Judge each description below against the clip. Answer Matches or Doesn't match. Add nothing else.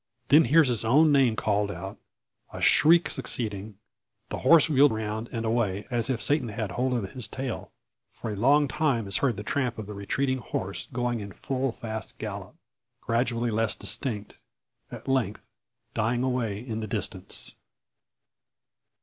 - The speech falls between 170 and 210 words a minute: Doesn't match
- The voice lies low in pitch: Matches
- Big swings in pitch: Doesn't match